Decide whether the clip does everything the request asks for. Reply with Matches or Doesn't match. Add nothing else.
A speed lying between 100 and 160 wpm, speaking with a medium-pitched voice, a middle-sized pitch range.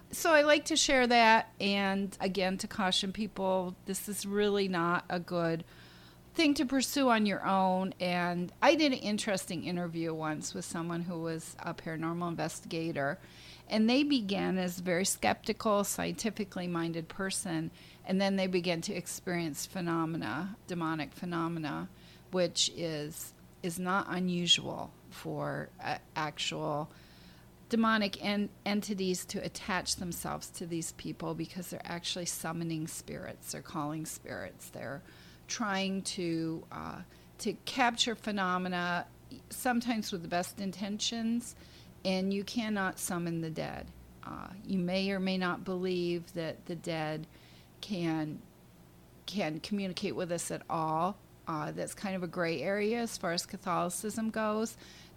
Matches